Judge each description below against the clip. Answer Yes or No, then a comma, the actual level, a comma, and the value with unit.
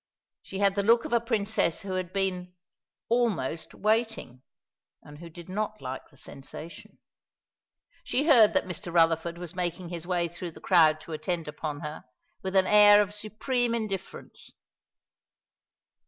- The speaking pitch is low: No, medium, 185 Hz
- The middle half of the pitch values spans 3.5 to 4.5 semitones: Yes, average, 4.1 semitones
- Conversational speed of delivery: Yes, average, 155 wpm